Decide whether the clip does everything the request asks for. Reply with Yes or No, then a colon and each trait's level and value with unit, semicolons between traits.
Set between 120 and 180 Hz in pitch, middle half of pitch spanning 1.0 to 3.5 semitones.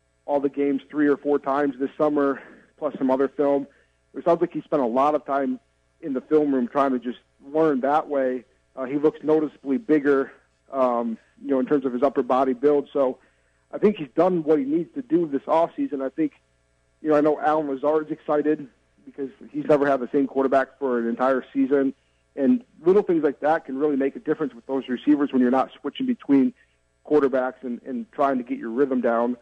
Yes: medium, 140 Hz; average, 2.9 semitones